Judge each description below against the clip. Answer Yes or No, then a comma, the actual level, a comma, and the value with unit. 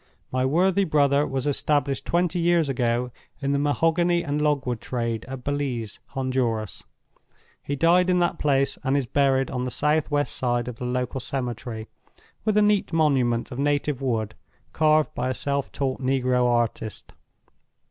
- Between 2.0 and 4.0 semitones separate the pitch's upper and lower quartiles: Yes, average, 3.3 semitones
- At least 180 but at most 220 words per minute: No, average, 160 wpm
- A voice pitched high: No, low, 135 Hz